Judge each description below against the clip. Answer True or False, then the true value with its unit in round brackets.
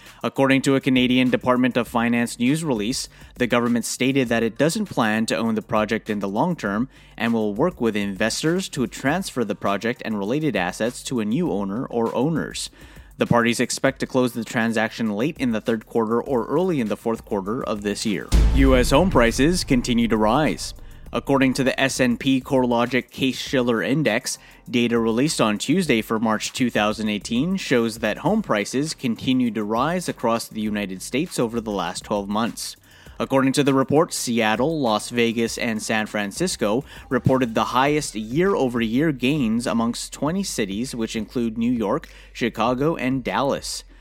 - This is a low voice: True (120 Hz)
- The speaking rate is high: False (170 wpm)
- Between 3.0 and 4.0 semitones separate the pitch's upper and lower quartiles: True (3.3 semitones)